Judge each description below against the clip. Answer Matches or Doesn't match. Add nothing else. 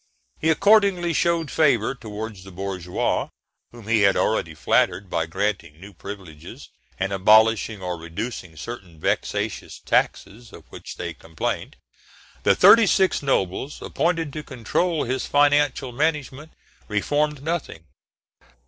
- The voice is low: Matches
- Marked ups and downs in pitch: Matches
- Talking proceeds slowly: Matches